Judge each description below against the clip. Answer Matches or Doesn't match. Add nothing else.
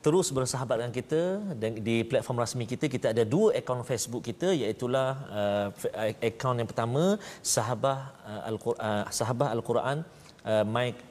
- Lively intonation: Doesn't match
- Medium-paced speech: Doesn't match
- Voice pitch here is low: Matches